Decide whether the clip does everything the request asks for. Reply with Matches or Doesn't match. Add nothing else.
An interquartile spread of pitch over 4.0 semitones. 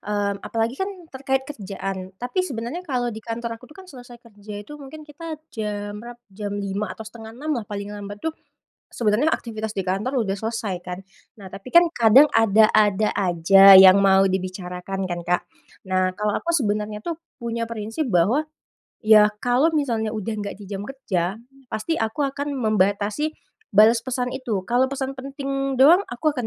Matches